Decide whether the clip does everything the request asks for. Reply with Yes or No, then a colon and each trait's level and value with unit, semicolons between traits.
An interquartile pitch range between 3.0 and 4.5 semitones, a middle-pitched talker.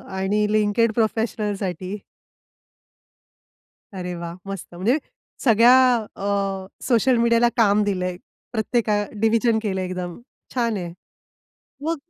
No: average, 3.5 semitones; high, 210 Hz